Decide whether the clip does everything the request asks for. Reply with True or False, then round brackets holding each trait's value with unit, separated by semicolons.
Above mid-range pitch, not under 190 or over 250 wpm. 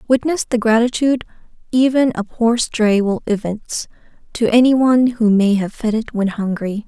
False (225 Hz; 165 wpm)